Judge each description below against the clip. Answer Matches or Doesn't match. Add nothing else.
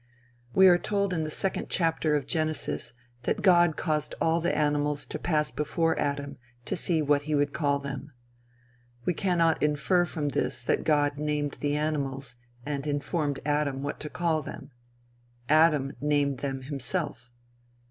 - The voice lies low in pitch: Doesn't match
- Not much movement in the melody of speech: Matches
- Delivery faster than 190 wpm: Doesn't match